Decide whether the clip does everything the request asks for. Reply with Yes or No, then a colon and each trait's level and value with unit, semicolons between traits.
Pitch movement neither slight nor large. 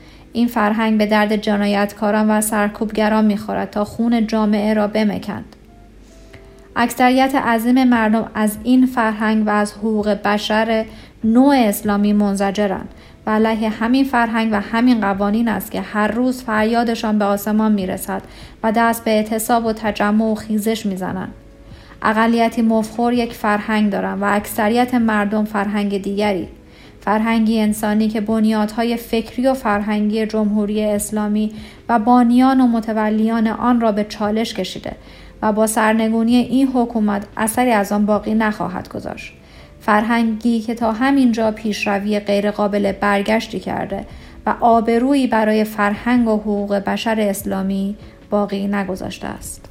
No: narrow, 1.7 semitones